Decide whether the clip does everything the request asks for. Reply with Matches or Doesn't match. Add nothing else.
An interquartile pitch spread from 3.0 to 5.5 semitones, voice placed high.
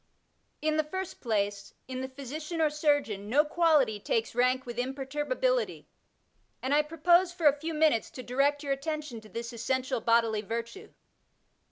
Matches